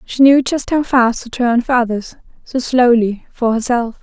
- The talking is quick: No, average, 195 wpm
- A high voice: Yes, high, 245 Hz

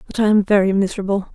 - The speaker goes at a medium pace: No, fast, 225 wpm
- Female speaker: Yes, female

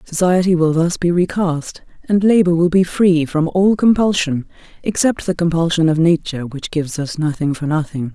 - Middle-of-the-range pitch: Yes, medium, 170 Hz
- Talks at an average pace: Yes, average, 175 wpm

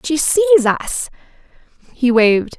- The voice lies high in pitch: Yes, very high, 285 Hz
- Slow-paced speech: Yes, slow, 115 wpm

